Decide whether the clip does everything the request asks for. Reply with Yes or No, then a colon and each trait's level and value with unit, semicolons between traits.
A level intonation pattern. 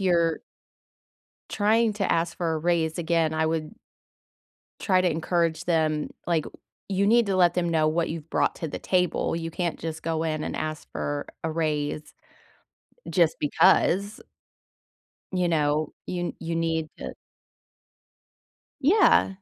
Yes: narrow, 2.2 semitones